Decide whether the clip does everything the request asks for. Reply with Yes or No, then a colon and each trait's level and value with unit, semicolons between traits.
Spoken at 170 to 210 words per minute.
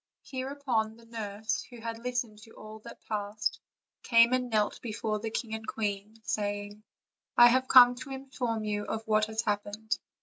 Yes: average, 175 wpm